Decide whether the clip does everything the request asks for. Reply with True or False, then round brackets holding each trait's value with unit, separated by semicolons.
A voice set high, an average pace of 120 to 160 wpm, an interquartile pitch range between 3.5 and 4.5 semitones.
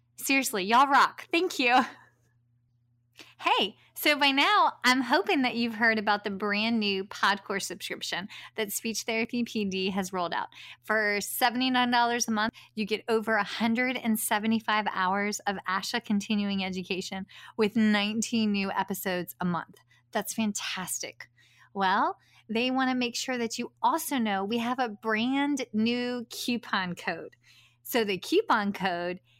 True (220 Hz; 140 wpm; 3.9 semitones)